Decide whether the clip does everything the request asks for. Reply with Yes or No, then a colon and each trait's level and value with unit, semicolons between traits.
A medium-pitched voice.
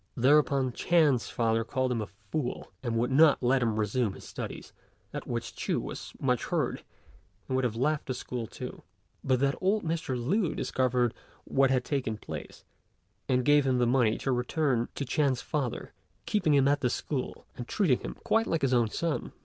No: low, 130 Hz